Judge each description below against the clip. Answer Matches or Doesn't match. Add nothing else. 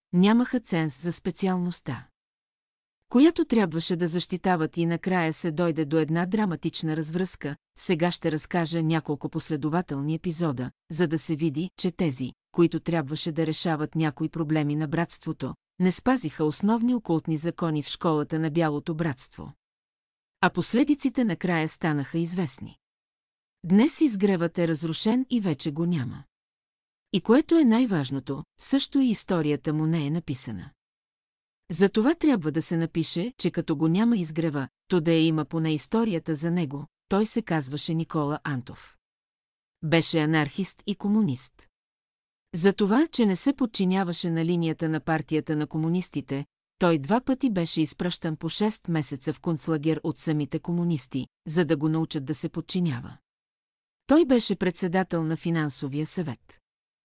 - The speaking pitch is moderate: Matches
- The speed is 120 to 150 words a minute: Matches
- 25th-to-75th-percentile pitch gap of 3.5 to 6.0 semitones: Doesn't match